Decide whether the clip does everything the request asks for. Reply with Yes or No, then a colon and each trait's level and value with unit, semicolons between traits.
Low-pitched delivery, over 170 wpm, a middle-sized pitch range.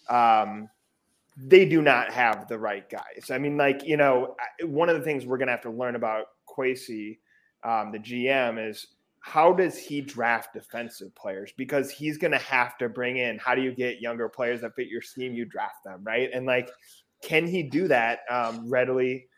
Yes: low, 125 Hz; average, 200 wpm; average, 3.1 semitones